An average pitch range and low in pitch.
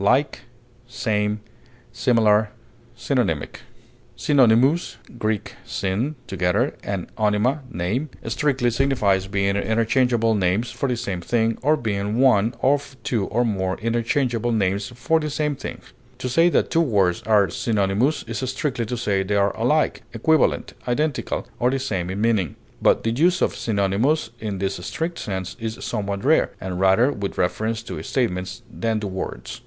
Yes: average, 4.5 semitones; low, 115 Hz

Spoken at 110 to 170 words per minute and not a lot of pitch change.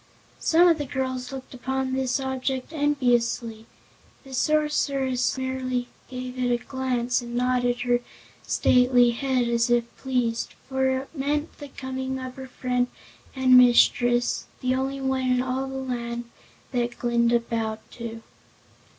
Yes: average, 140 wpm; narrow, 1.5 semitones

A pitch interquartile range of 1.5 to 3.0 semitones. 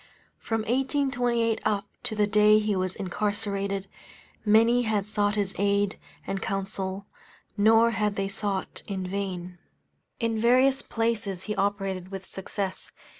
Yes: narrow, 2.4 semitones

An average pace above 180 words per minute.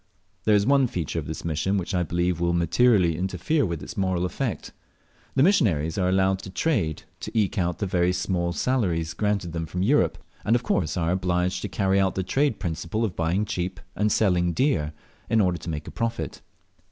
Yes: average, 200 wpm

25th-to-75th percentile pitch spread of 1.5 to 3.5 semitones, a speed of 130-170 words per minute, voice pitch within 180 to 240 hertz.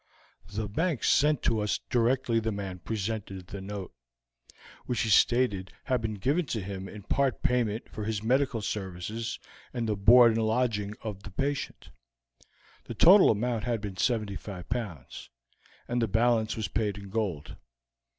No: average, 3.2 semitones; average, 160 wpm; low, 110 Hz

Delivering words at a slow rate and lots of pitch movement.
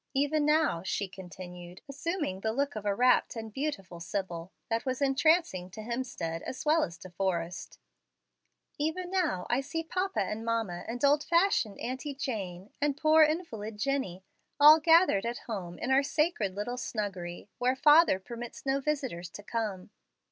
No: average, 160 wpm; wide, 7.6 semitones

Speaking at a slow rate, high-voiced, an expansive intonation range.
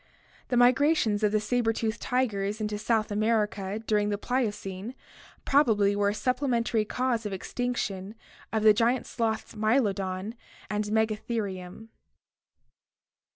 No: slow, 125 wpm; high, 220 Hz; narrow, 2.5 semitones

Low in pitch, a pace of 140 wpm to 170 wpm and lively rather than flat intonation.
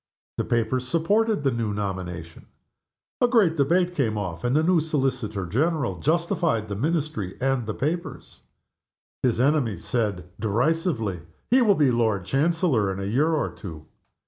Yes: low, 130 Hz; average, 150 wpm; wide, 7.7 semitones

